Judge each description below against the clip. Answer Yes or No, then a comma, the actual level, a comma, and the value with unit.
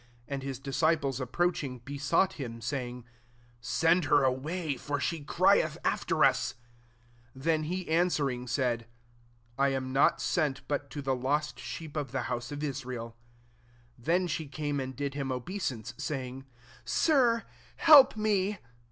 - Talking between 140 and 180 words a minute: Yes, average, 145 wpm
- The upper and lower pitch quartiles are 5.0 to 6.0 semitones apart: No, average, 3.8 semitones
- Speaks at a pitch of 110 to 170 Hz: Yes, medium, 140 Hz